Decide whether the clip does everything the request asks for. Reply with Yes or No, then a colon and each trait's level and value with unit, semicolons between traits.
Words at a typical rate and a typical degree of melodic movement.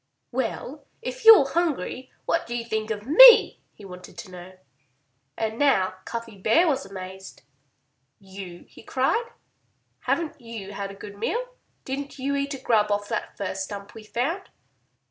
No: average, 160 wpm; wide, 6.1 semitones